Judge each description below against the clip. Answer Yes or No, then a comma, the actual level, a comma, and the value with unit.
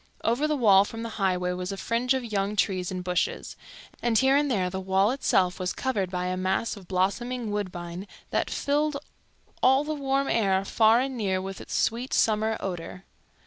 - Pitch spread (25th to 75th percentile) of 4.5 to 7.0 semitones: Yes, average, 4.9 semitones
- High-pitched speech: Yes, high, 205 Hz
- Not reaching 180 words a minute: No, average, 190 wpm